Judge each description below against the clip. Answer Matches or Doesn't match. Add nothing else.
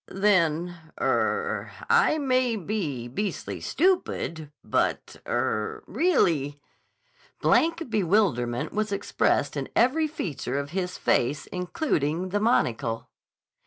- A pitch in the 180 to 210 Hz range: Matches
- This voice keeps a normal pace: Doesn't match